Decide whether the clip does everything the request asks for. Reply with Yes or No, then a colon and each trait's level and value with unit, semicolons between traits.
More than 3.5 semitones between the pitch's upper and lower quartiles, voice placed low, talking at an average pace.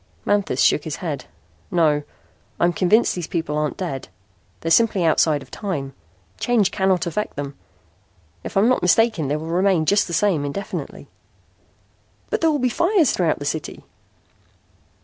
No: average, 5.0 semitones; medium, 175 Hz; average, 155 wpm